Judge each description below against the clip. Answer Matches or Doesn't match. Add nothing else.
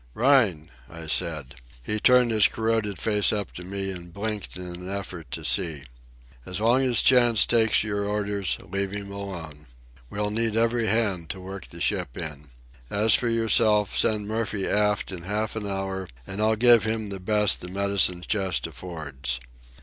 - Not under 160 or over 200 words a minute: Matches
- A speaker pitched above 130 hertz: Doesn't match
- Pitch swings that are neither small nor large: Matches